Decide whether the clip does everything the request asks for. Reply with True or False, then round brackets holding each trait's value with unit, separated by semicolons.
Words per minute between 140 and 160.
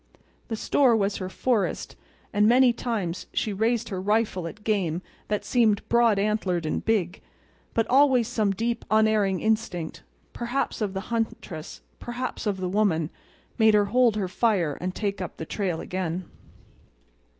True (150 wpm)